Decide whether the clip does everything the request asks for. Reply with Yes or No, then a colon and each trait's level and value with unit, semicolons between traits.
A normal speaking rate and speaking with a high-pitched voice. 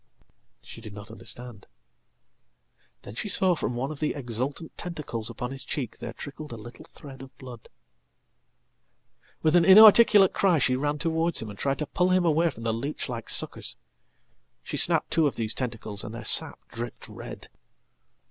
No: average, 165 wpm; low, 135 Hz